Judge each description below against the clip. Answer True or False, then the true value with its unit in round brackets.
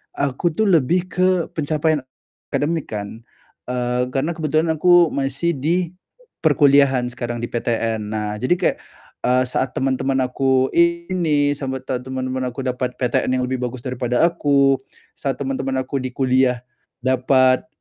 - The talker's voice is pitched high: False (135 Hz)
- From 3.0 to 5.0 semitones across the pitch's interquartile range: True (3.6 semitones)